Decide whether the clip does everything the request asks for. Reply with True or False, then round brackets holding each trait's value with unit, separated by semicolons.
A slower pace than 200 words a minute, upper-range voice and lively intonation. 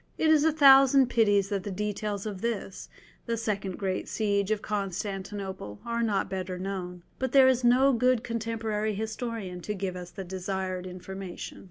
False (170 wpm; 205 Hz; 3.4 semitones)